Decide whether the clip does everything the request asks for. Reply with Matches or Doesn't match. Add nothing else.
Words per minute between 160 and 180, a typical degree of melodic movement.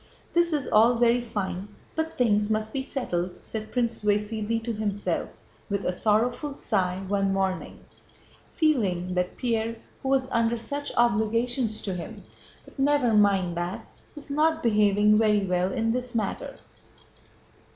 Doesn't match